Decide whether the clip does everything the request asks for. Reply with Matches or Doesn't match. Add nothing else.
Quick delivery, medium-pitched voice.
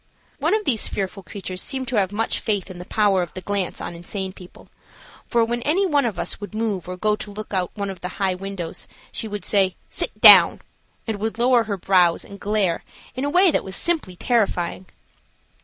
Doesn't match